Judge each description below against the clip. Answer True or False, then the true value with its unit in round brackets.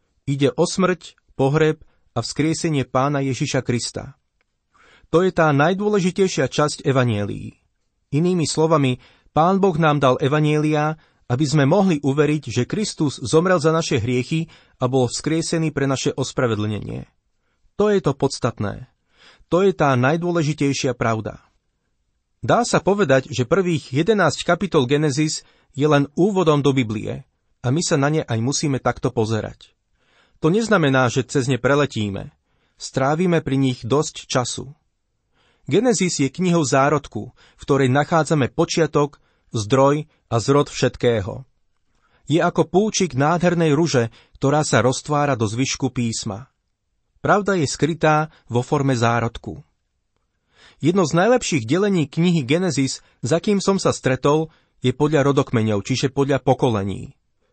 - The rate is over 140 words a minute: False (130 wpm)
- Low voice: False (145 Hz)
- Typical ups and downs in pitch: True (4.1 semitones)